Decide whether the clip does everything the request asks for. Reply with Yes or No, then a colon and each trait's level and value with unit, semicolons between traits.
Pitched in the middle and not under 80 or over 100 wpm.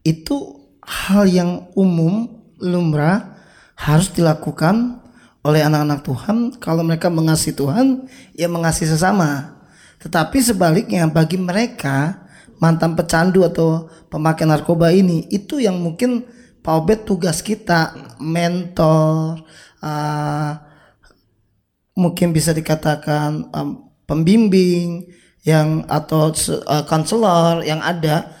Yes: medium, 165 Hz; average, 95 wpm